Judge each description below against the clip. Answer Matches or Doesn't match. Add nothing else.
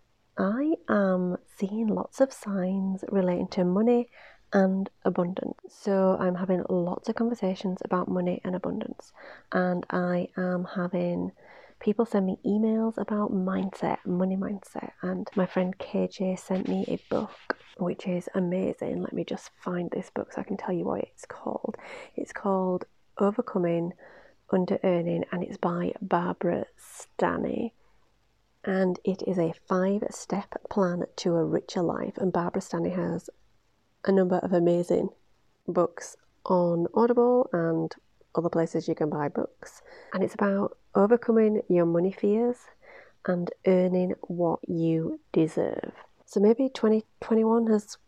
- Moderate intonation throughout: Matches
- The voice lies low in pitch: Doesn't match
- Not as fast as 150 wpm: Matches